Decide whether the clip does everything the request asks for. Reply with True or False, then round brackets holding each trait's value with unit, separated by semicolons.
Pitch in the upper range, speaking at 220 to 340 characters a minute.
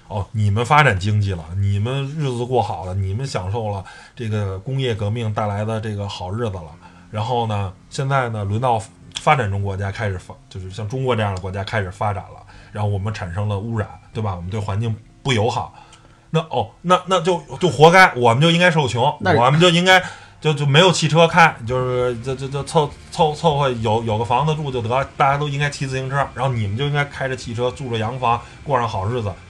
False (120 Hz; 325 characters per minute)